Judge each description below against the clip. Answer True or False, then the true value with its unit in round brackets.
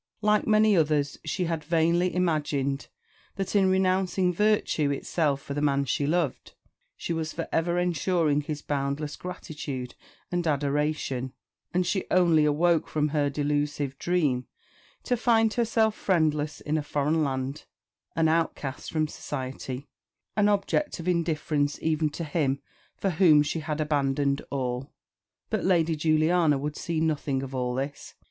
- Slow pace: False (145 wpm)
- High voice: False (155 Hz)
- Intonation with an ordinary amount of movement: True (3.6 semitones)